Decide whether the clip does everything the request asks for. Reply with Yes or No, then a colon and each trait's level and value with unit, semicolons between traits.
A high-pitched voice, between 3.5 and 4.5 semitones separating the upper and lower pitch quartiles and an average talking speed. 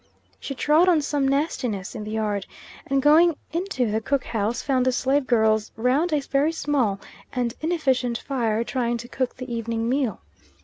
Yes: very high, 255 Hz; average, 4.1 semitones; average, 175 wpm